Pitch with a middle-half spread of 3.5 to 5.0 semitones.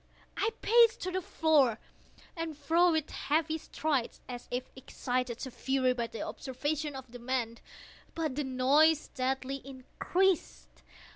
Yes: average, 3.8 semitones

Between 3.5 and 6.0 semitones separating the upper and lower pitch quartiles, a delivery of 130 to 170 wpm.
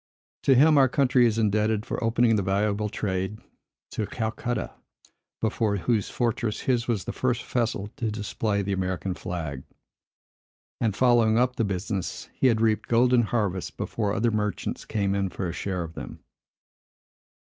No: average, 3.1 semitones; average, 160 wpm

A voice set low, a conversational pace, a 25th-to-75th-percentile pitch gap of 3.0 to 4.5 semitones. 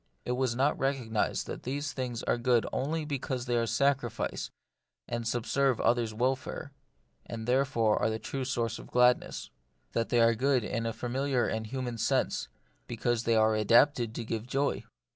No: low, 120 Hz; average, 170 wpm; narrow, 2.5 semitones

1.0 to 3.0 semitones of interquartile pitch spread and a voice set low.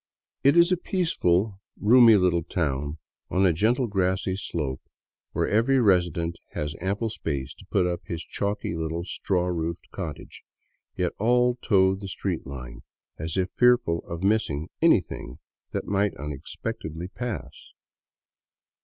No: average, 4.8 semitones; very low, 90 Hz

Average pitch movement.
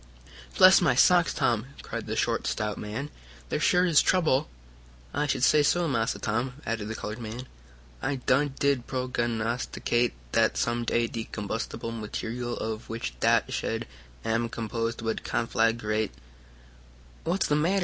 Yes: average, 3.3 semitones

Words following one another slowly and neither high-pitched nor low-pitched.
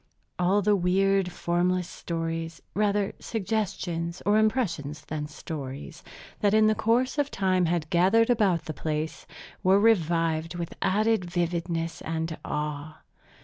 Yes: slow, 130 wpm; medium, 175 Hz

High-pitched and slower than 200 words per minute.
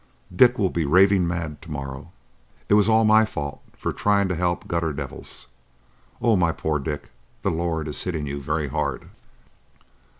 No: very low, 85 Hz; average, 170 wpm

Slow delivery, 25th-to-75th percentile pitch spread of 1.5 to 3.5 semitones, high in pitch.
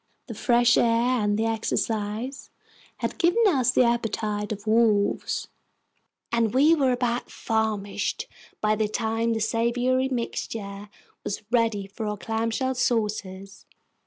Yes: slow, 130 wpm; average, 2.7 semitones; high, 225 Hz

